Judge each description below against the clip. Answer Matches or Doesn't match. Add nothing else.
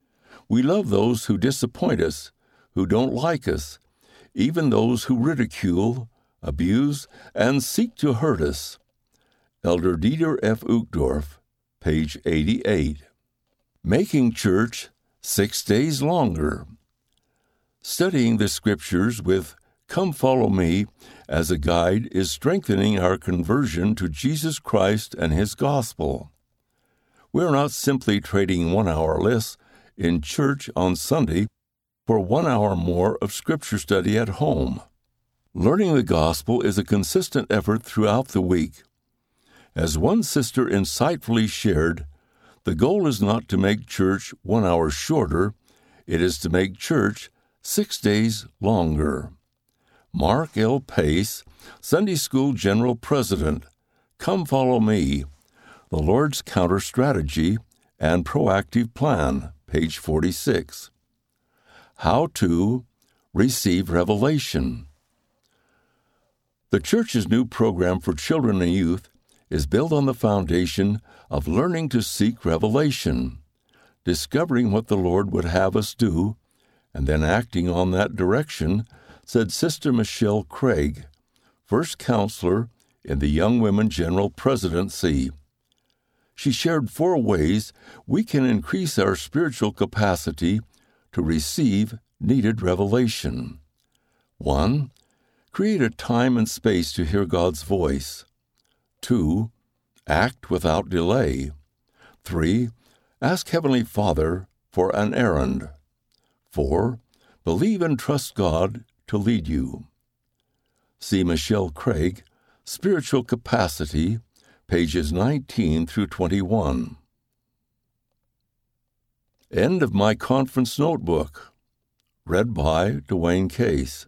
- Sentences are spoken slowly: Matches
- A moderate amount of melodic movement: Doesn't match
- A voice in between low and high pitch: Doesn't match